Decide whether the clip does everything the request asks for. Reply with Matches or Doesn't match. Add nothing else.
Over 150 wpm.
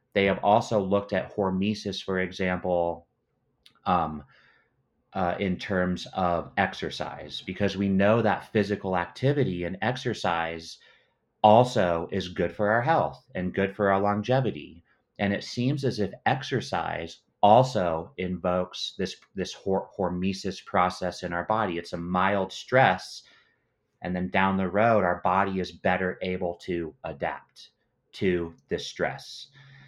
Doesn't match